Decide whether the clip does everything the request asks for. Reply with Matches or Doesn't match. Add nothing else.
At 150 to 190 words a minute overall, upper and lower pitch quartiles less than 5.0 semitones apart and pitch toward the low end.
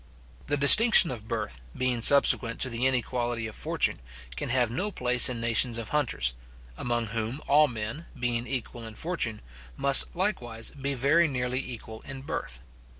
Matches